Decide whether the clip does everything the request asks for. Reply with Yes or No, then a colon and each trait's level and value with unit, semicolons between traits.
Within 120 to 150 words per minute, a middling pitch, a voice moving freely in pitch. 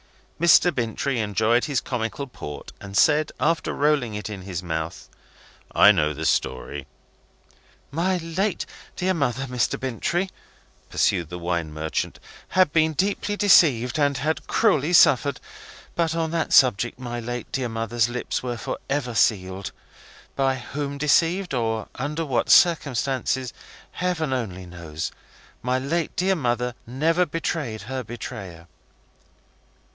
No: slow, 135 wpm; low, 130 Hz; wide, 6.4 semitones